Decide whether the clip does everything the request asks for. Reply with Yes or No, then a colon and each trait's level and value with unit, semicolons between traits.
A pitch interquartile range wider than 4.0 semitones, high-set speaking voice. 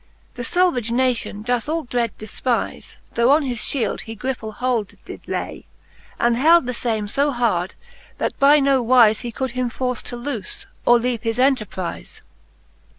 No: narrow, 2.6 semitones; high, 245 Hz